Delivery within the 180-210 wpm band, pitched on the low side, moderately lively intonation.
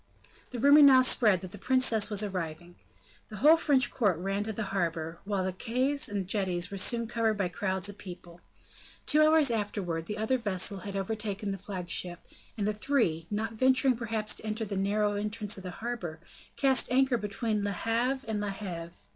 No: average, 190 wpm; high, 210 Hz; average, 3.6 semitones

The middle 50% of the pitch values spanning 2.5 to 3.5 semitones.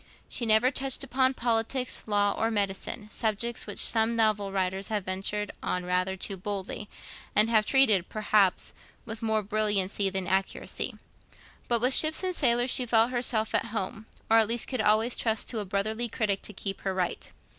Yes: average, 2.9 semitones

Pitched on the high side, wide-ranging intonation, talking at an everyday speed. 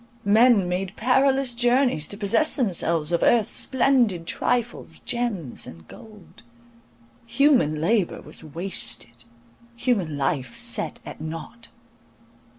No: high, 205 Hz; wide, 7.2 semitones; slow, 105 wpm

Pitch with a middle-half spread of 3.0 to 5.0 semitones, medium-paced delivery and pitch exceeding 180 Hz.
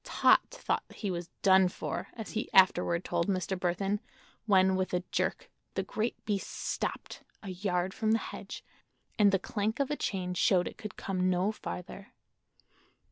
No: narrow, 2.5 semitones; average, 160 wpm; high, 190 Hz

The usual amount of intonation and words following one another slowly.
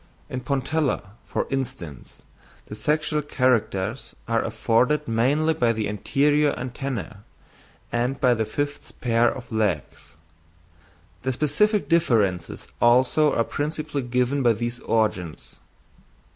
Yes: average, 4.3 semitones; slow, 115 wpm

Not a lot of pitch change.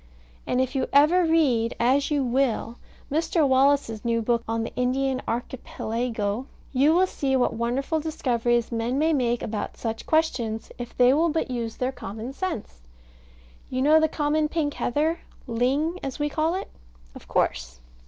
No: average, 4.3 semitones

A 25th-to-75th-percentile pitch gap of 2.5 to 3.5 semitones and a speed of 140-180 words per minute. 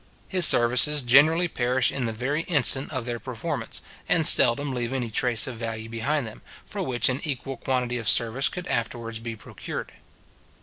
Yes: average, 2.9 semitones; average, 175 wpm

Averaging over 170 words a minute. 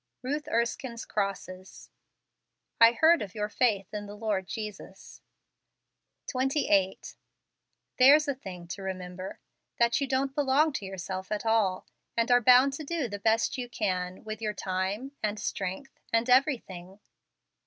No: average, 145 wpm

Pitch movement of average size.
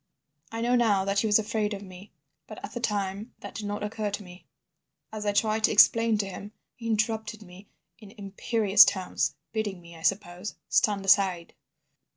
No: narrow, 1.9 semitones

